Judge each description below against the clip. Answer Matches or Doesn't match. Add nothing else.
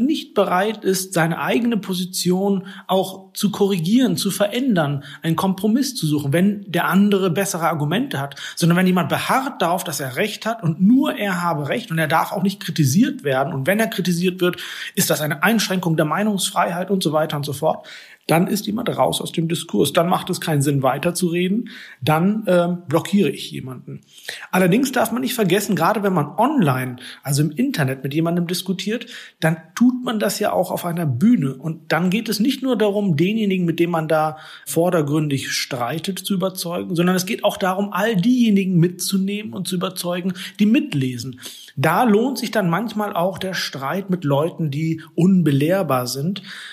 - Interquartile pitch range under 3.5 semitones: Doesn't match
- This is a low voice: Doesn't match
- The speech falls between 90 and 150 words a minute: Doesn't match